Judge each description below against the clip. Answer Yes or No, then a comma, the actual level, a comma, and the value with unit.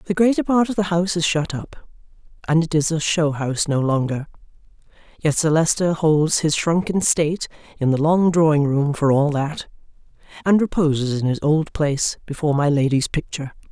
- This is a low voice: No, medium, 160 Hz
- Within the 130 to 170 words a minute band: No, average, 185 wpm